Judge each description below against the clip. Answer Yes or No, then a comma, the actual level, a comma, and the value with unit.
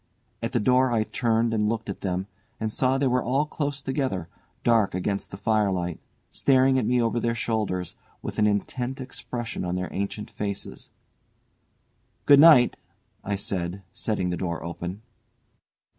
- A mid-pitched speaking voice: No, low, 110 Hz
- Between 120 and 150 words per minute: No, average, 160 wpm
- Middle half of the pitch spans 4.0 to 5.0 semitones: Yes, average, 4.6 semitones